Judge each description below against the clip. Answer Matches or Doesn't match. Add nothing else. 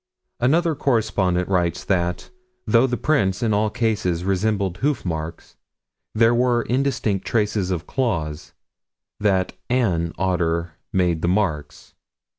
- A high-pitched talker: Doesn't match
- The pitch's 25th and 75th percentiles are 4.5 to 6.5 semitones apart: Matches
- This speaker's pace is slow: Matches